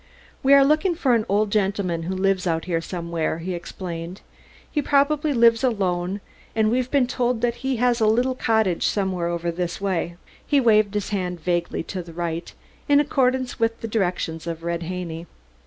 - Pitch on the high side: Yes, high, 200 Hz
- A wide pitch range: Yes, wide, 6.0 semitones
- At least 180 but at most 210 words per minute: Yes, average, 185 wpm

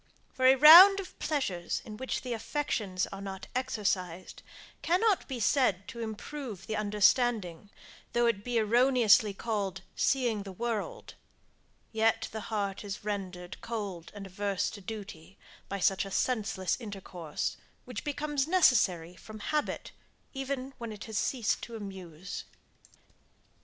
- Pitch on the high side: Yes, high, 215 Hz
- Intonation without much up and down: No, average, 4.7 semitones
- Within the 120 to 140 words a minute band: Yes, slow, 135 wpm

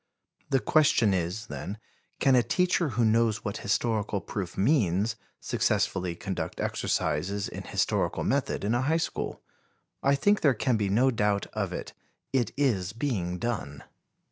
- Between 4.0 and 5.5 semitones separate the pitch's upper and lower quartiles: Yes, average, 5.1 semitones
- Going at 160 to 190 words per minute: No, average, 150 wpm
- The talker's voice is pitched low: Yes, low, 110 Hz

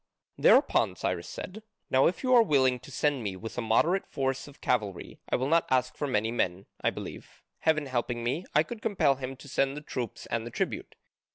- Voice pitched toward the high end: No, low, 130 Hz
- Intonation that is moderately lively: Yes, average, 4.1 semitones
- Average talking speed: No, fast, 210 wpm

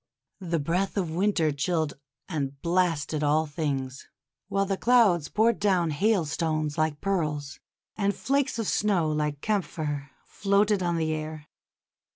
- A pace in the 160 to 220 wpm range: No, slow, 135 wpm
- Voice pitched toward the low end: No, medium, 165 Hz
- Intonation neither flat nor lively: Yes, average, 4.6 semitones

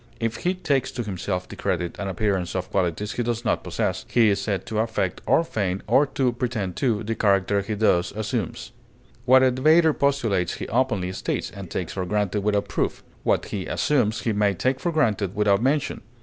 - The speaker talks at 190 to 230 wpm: Yes, average, 200 wpm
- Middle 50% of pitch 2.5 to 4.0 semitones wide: No, average, 4.4 semitones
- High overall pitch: No, low, 105 Hz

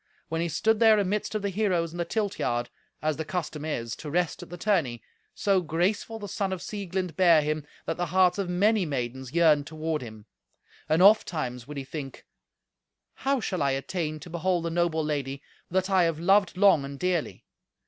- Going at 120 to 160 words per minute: No, average, 200 wpm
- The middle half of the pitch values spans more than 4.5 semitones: No, average, 4.0 semitones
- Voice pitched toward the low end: No, medium, 170 Hz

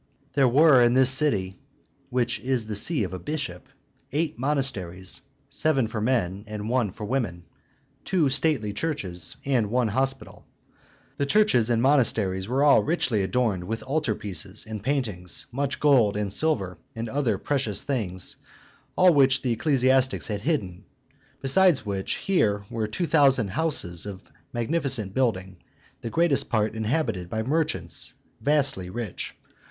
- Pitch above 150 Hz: No, low, 120 Hz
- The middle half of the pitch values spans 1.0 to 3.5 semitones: No, wide, 5.4 semitones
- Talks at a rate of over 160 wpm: No, average, 145 wpm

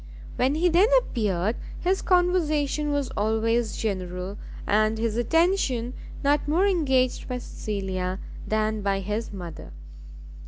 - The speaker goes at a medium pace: No, slow, 120 wpm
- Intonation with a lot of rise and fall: Yes, wide, 6.4 semitones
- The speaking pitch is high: Yes, high, 230 Hz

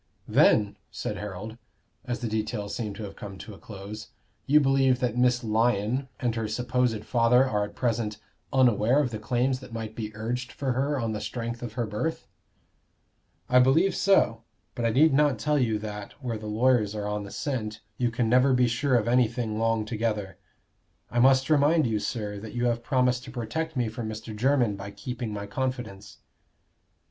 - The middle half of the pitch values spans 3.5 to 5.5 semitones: No, average, 2.9 semitones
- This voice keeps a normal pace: Yes, average, 190 wpm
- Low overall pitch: Yes, low, 115 Hz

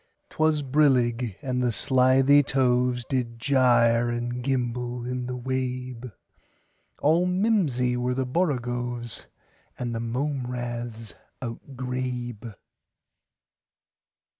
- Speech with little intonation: Yes, narrow, 1.5 semitones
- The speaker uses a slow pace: Yes, slow, 90 wpm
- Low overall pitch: Yes, low, 125 Hz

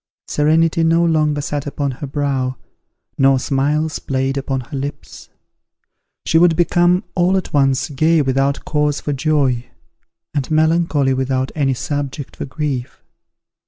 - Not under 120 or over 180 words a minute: Yes, slow, 135 wpm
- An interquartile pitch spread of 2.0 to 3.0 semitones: Yes, average, 2.7 semitones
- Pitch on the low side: No, medium, 145 Hz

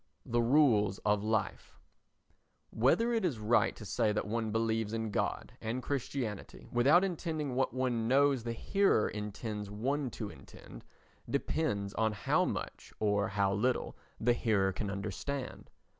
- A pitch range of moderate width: Yes, average, 4.1 semitones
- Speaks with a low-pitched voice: Yes, low, 115 Hz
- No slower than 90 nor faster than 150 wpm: Yes, average, 145 wpm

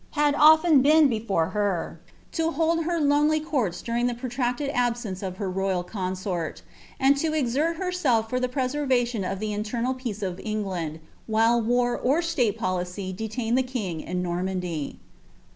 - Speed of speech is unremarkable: Yes, average, 165 wpm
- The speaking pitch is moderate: No, high, 235 Hz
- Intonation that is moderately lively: No, wide, 6.6 semitones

